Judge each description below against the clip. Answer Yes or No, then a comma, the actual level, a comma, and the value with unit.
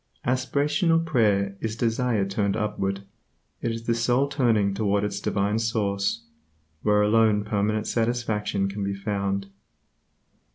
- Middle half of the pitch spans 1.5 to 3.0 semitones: Yes, average, 2.7 semitones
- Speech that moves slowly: Yes, slow, 130 wpm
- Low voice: Yes, low, 105 Hz